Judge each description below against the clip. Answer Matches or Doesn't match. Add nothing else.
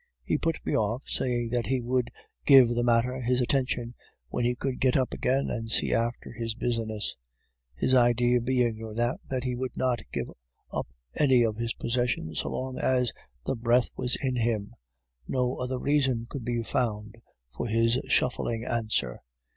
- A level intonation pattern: Matches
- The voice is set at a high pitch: Doesn't match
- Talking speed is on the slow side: Doesn't match